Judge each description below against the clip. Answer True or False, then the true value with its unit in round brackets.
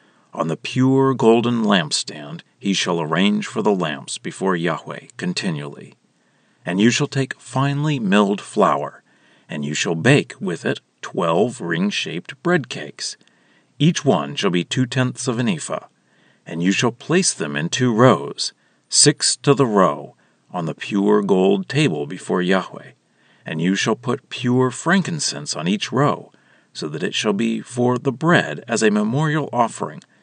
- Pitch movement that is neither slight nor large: False (5.9 semitones)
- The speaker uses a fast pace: False (160 wpm)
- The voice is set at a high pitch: False (135 Hz)